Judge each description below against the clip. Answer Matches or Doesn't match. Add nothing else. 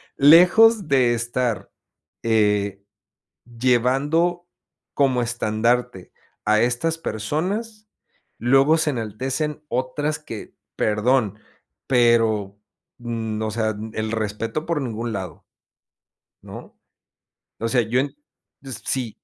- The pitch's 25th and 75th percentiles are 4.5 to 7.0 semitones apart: Matches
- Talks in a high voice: Doesn't match